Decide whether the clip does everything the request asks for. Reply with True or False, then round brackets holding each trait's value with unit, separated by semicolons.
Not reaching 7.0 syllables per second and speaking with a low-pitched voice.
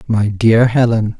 True (3.9 syllables/s; 110 Hz)